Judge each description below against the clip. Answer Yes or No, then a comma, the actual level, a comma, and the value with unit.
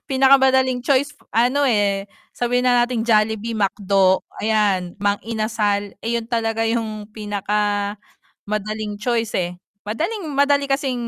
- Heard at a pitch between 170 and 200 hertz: No, high, 225 Hz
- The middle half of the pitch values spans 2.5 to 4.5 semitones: Yes, average, 3.4 semitones